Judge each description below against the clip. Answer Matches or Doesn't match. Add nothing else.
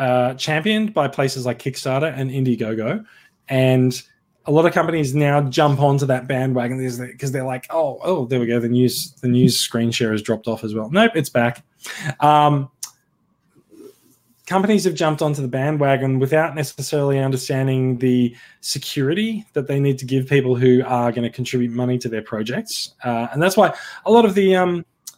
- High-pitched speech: Doesn't match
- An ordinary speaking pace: Matches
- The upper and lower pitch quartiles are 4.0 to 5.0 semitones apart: Doesn't match